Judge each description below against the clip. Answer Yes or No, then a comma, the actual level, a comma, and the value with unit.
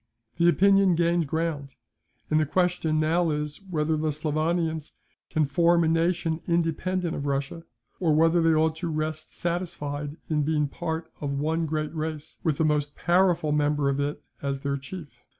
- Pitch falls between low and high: Yes, medium, 160 Hz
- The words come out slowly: No, average, 170 wpm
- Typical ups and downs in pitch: No, narrow, 2.2 semitones